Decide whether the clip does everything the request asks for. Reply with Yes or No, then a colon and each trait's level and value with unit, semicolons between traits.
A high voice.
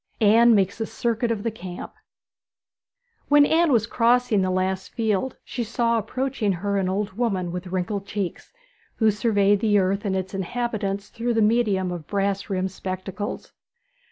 Yes: high, 205 Hz